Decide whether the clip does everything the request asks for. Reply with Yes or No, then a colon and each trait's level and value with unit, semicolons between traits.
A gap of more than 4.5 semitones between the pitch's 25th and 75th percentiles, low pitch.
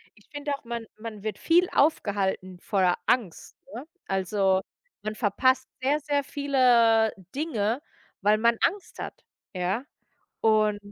No: average, 5.0 semitones; high, 225 Hz